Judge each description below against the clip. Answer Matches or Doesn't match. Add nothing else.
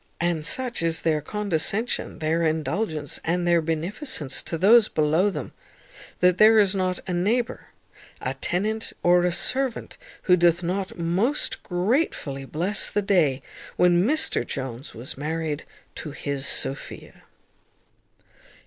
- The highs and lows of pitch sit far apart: Doesn't match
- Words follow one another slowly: Matches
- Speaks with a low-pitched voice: Doesn't match